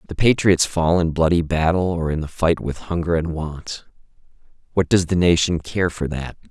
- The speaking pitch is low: Yes, very low, 85 Hz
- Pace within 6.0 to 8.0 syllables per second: No, 4.9 syllables/s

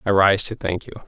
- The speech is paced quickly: Yes, fast, 280 wpm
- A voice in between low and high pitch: No, low, 100 Hz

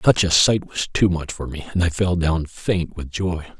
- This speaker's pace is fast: Yes, fast, 250 wpm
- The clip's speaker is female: No, male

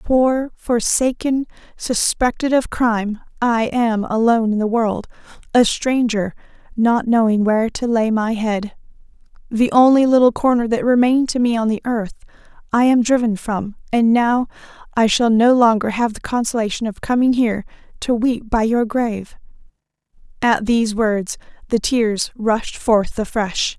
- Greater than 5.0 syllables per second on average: No, 4.6 syllables/s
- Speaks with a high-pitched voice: Yes, high, 230 Hz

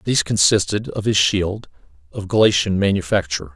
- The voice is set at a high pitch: No, very low, 95 Hz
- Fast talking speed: No, slow, 135 wpm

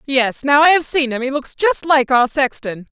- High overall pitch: Yes, very high, 275 Hz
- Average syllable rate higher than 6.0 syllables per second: No, 5.1 syllables/s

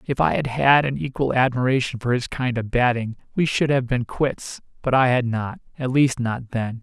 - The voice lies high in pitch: No, low, 125 Hz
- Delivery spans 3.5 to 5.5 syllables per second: Yes, 4.9 syllables/s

